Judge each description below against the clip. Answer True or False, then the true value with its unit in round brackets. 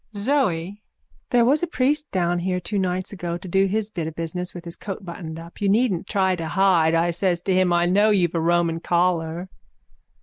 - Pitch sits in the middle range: True (180 Hz)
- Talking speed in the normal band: False (210 wpm)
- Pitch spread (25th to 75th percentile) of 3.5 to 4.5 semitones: False (2.7 semitones)